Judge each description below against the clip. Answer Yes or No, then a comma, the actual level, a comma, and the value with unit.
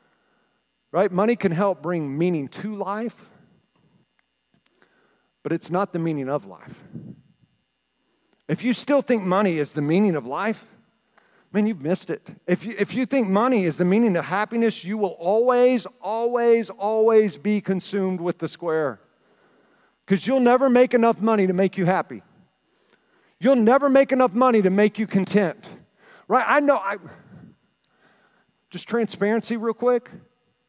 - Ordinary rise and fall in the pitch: Yes, average, 3.8 semitones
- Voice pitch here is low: No, high, 210 Hz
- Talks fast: No, average, 150 wpm